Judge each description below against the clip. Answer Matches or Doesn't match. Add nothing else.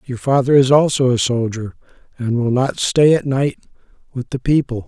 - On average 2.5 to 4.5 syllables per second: Doesn't match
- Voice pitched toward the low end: Matches